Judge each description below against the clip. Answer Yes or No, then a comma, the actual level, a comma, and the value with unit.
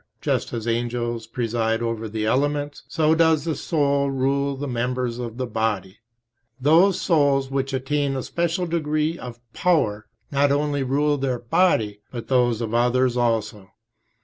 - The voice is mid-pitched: No, low, 130 Hz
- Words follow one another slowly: No, average, 155 wpm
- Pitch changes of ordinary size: Yes, average, 3.8 semitones